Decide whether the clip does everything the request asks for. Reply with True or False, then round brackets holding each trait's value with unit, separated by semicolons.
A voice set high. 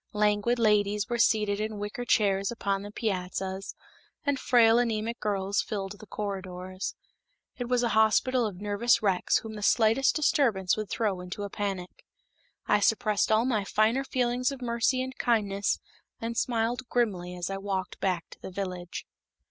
True (210 Hz)